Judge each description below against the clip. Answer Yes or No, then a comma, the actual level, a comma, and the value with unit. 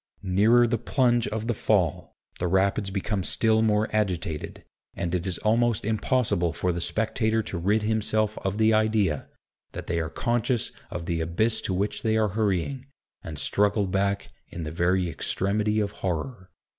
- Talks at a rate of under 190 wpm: Yes, average, 170 wpm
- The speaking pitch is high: No, low, 105 Hz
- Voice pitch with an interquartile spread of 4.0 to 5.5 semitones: No, average, 3.4 semitones